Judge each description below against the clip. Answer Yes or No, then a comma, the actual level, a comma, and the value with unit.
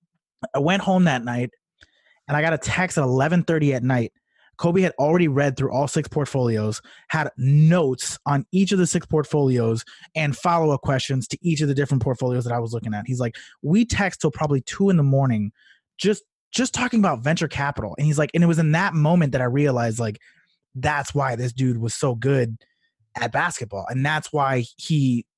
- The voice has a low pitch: No, medium, 145 Hz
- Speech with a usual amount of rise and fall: Yes, average, 4.5 semitones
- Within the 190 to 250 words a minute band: Yes, fast, 205 wpm